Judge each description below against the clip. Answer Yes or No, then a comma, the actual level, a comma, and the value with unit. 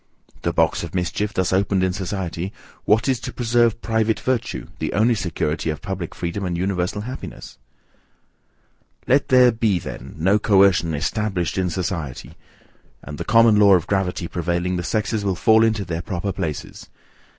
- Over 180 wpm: No, average, 160 wpm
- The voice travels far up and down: No, average, 3.9 semitones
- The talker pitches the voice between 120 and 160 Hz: No, very low, 95 Hz